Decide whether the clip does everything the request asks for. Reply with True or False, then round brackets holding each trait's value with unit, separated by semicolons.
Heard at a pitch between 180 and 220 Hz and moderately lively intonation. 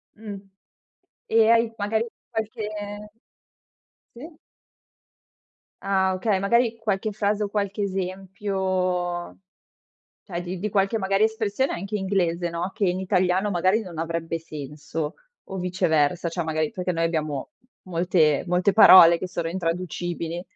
True (185 Hz; 3.0 semitones)